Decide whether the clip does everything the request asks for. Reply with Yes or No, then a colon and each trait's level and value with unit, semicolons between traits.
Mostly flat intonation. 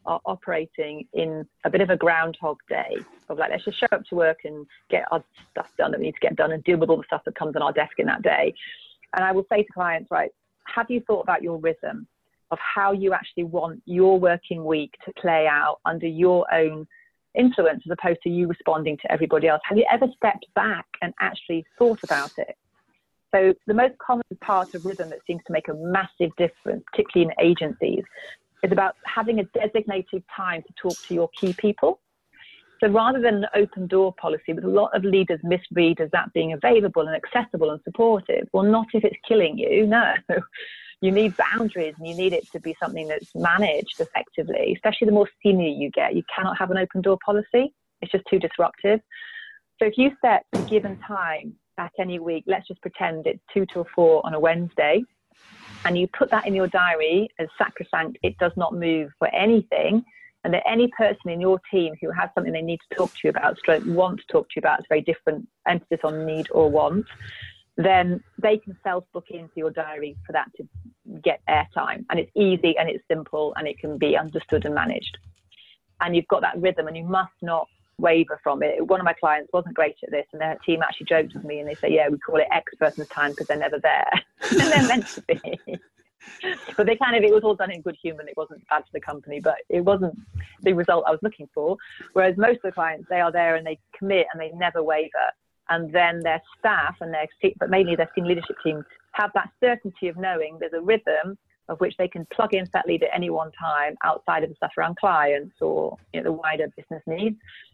No: average, 4.4 semitones